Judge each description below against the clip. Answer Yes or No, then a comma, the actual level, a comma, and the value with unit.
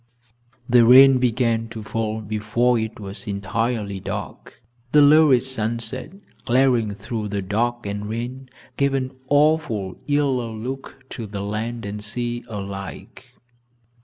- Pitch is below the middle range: Yes, low, 115 Hz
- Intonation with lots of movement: No, average, 3.5 semitones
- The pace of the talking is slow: Yes, slow, 130 wpm